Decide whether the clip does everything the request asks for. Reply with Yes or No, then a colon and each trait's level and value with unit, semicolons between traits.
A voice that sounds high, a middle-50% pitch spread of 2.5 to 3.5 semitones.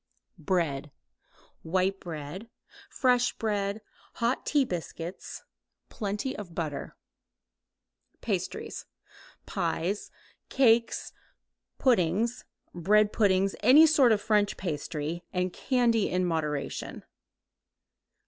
No: high, 195 Hz; average, 5.2 semitones